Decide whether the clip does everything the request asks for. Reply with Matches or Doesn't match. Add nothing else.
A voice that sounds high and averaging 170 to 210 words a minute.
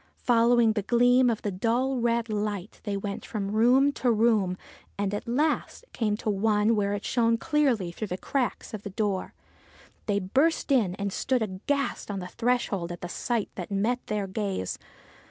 Matches